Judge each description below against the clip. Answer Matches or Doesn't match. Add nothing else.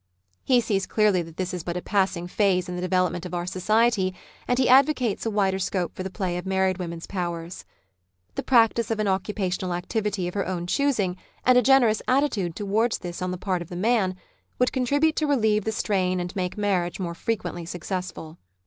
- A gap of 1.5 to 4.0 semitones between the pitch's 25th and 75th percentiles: Matches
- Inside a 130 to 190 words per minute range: Doesn't match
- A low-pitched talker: Doesn't match